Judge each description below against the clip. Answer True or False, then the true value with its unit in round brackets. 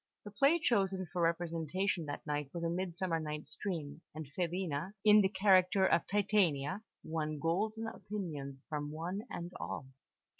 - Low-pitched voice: False (175 Hz)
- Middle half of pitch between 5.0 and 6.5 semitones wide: False (4.0 semitones)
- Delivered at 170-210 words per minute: False (150 wpm)